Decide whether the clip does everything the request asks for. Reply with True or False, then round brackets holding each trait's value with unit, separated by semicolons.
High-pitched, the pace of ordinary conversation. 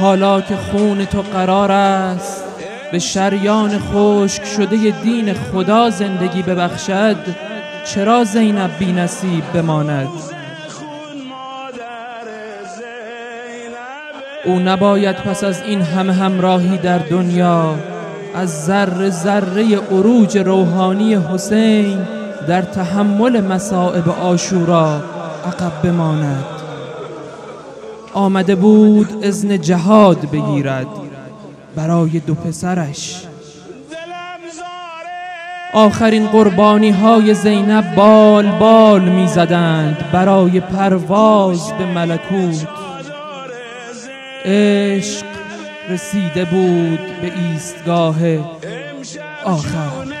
False (195 Hz; 80 wpm)